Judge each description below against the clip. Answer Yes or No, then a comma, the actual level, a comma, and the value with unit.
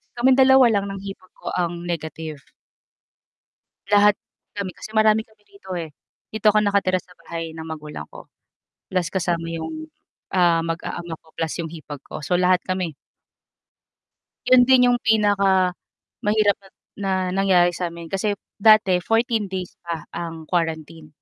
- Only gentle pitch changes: No, average, 3.8 semitones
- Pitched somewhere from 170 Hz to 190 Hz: Yes, medium, 185 Hz